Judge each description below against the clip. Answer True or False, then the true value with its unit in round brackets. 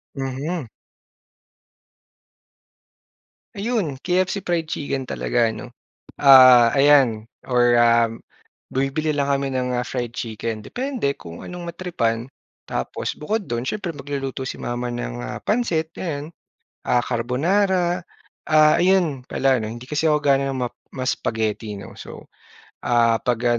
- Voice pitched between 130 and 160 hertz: True (135 Hz)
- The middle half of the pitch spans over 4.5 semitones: True (4.9 semitones)